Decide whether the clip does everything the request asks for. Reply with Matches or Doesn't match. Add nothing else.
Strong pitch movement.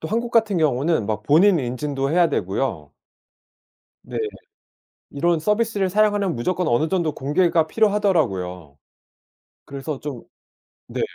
Matches